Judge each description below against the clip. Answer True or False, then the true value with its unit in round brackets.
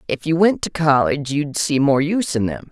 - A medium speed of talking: False (245 wpm)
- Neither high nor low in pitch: True (150 Hz)